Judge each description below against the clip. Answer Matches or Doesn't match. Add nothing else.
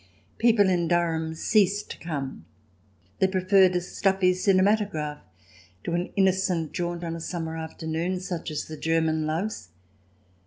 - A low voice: Doesn't match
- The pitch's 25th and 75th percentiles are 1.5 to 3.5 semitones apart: Matches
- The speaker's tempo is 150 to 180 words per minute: Doesn't match